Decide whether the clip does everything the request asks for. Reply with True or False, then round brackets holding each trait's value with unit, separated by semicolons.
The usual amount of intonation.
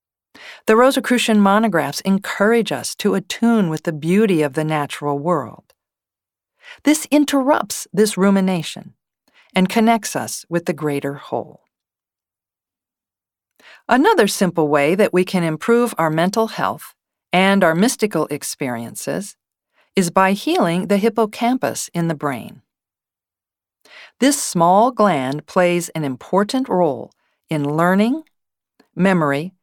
False (6.1 semitones)